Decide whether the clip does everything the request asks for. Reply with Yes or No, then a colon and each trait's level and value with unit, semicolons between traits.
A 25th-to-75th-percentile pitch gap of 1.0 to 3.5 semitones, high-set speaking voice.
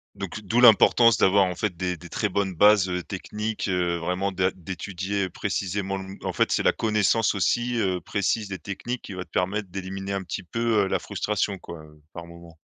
No: narrow, 2.4 semitones; very low, 95 Hz